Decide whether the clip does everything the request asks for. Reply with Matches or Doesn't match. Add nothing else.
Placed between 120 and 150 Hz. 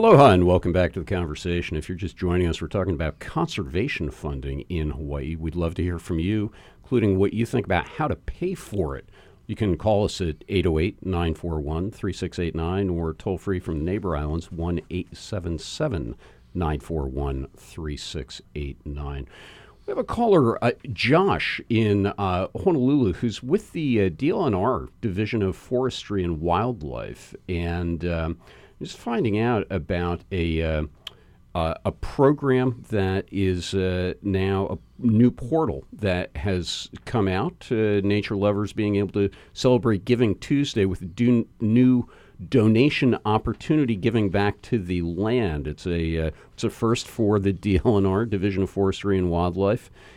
Doesn't match